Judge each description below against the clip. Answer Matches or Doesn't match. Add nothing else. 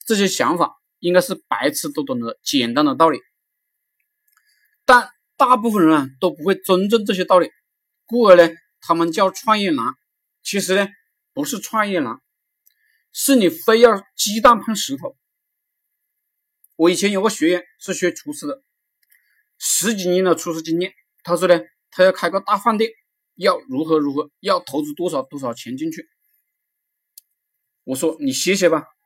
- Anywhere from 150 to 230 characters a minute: Matches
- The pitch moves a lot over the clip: Matches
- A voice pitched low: Doesn't match